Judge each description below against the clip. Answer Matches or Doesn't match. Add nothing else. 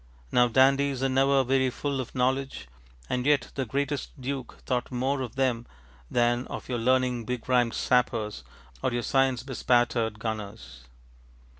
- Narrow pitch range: Matches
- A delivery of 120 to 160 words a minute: Matches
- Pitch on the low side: Matches